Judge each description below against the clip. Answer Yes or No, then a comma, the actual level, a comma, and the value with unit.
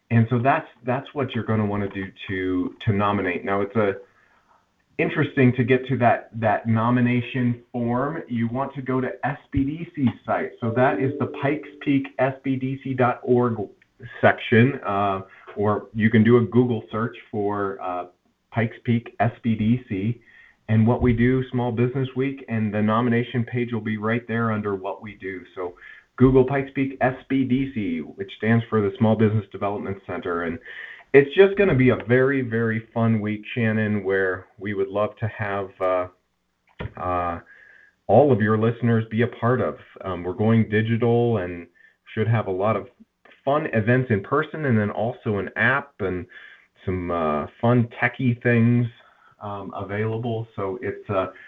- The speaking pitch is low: Yes, low, 115 Hz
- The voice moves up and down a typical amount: Yes, average, 3.4 semitones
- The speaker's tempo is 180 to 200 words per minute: No, average, 165 wpm